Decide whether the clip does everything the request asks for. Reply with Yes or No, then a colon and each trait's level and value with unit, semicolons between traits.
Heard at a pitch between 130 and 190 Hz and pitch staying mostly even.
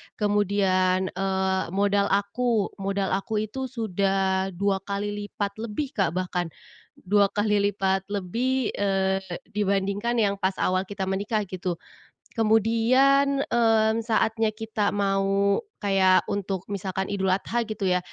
No: high, 200 Hz; narrow, 2.2 semitones